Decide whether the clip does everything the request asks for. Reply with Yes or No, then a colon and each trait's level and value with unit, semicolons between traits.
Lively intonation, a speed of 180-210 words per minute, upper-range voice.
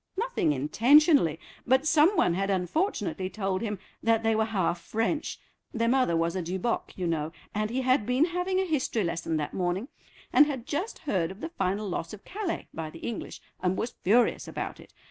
Yes: wide, 8.0 semitones; average, 185 wpm; high, 220 Hz